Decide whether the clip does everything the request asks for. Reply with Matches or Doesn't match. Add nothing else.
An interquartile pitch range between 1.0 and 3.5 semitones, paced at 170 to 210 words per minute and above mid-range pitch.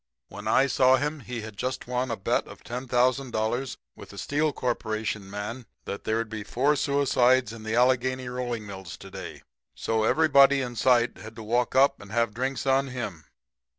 Doesn't match